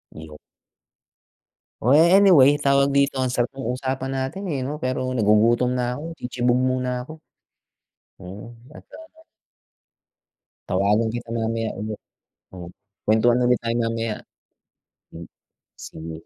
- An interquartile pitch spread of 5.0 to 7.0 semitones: No, average, 3.2 semitones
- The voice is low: Yes, low, 125 Hz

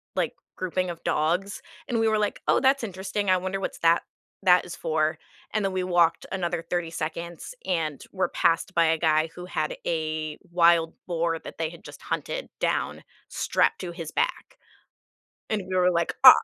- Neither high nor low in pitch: Yes, medium, 175 Hz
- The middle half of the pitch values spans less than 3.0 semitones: Yes, narrow, 2.4 semitones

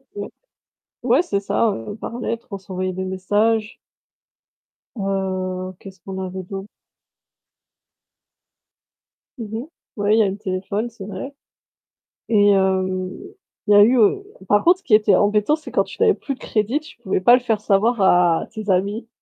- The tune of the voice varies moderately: Yes, average, 3.2 semitones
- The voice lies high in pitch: Yes, high, 205 Hz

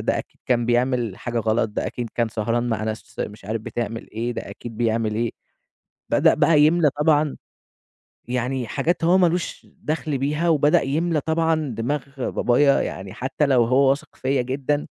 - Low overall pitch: Yes, low, 130 Hz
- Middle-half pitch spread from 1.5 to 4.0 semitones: No, average, 4.4 semitones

